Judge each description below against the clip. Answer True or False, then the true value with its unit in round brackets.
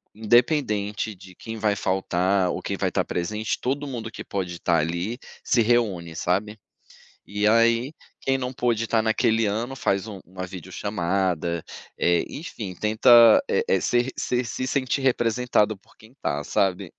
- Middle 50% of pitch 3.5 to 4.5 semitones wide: True (4.2 semitones)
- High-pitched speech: False (110 Hz)